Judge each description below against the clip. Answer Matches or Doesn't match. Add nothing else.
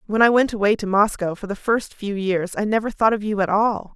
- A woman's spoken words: Matches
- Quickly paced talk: Matches